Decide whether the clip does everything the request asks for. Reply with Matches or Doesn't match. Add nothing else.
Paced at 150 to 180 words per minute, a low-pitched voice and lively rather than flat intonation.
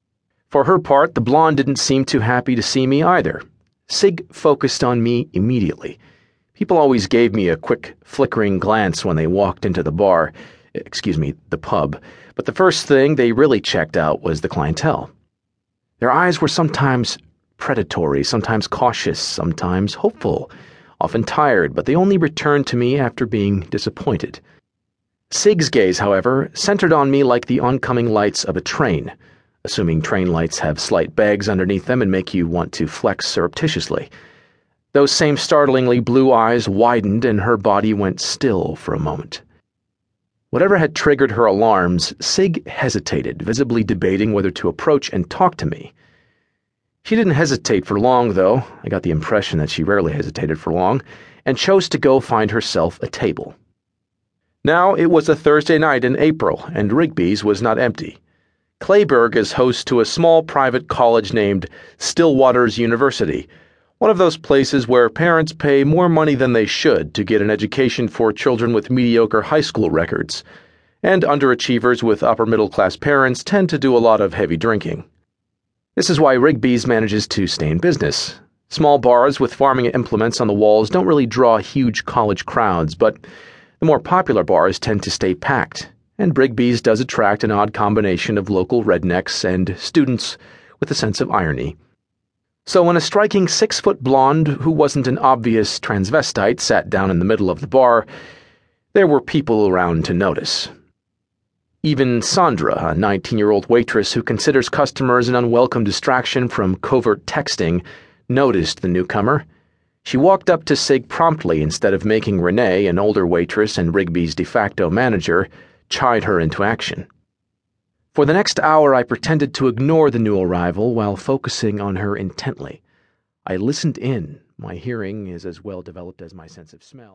Matches